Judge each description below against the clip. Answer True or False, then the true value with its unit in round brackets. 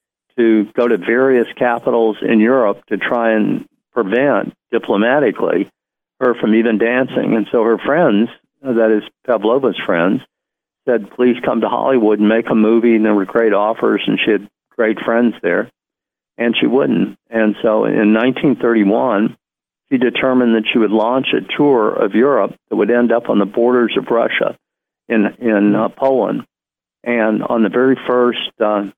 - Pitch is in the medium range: False (115 Hz)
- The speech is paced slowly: False (165 wpm)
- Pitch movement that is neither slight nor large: False (1.9 semitones)